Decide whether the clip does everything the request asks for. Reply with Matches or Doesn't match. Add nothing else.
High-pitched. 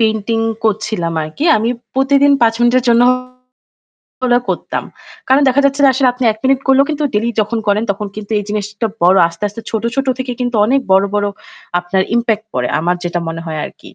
Matches